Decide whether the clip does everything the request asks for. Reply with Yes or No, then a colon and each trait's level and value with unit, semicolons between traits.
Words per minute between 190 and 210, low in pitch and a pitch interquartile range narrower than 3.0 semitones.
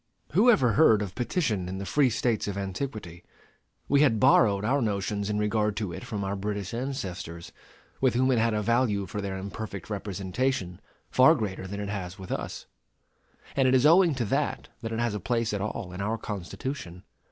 No: average, 195 wpm; low, 105 Hz; average, 4.2 semitones